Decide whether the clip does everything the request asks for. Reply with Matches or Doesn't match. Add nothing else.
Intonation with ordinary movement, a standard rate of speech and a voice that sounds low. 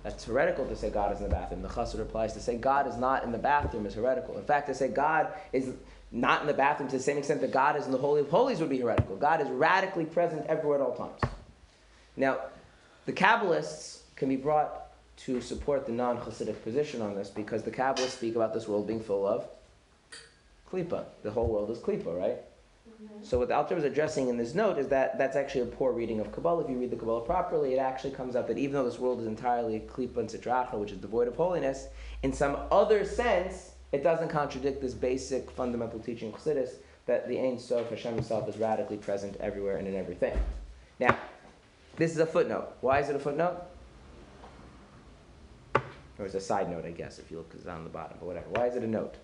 Doesn't match